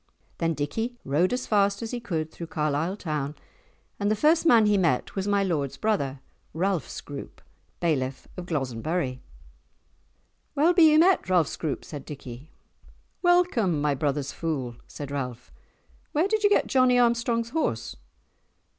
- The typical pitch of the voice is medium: Yes, medium, 175 Hz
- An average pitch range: No, wide, 8.4 semitones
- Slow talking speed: No, average, 150 wpm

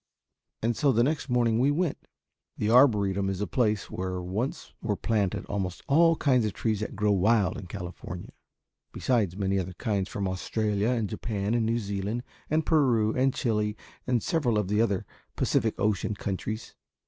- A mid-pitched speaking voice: No, low, 110 Hz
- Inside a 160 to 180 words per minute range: Yes, average, 175 wpm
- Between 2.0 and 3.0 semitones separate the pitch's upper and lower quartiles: No, average, 3.5 semitones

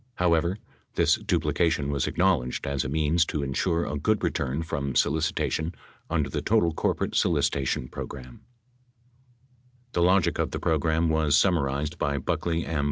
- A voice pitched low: Yes, very low, 80 Hz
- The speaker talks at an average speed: Yes, average, 150 wpm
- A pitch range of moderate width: Yes, average, 3.2 semitones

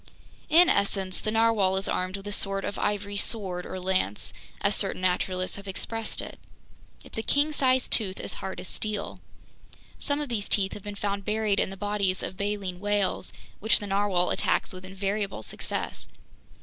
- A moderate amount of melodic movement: No, narrow, 2.0 semitones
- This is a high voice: Yes, high, 200 Hz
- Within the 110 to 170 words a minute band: No, average, 180 wpm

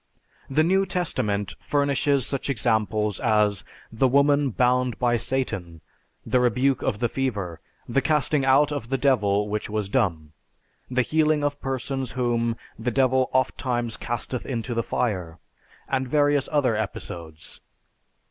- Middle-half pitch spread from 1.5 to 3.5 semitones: No, average, 4.1 semitones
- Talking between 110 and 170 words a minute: Yes, average, 140 wpm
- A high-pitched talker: No, low, 125 Hz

